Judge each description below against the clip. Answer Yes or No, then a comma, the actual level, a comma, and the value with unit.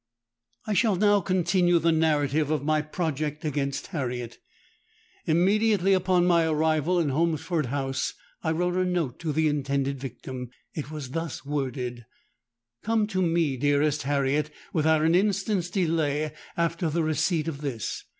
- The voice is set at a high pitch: No, medium, 155 Hz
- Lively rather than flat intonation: No, average, 3.8 semitones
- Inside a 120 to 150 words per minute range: Yes, average, 140 wpm